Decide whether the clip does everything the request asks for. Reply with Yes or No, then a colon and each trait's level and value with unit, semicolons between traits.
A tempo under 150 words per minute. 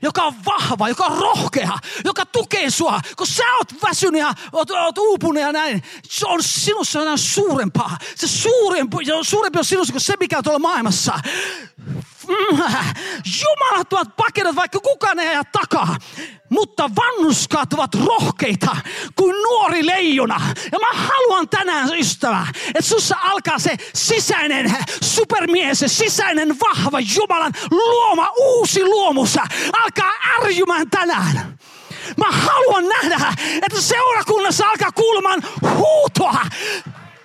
Yes: average, 125 wpm